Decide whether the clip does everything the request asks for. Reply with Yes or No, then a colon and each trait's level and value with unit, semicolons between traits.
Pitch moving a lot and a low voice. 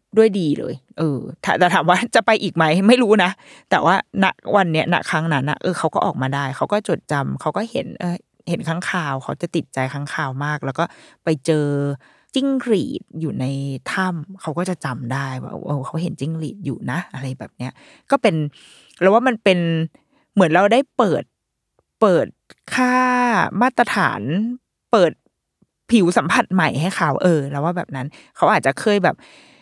No: wide, 6.1 semitones; medium, 175 Hz